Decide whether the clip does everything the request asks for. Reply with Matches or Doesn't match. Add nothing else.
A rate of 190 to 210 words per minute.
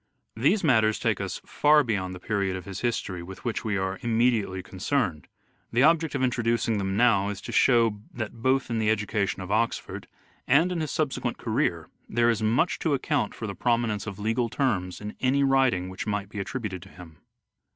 Matches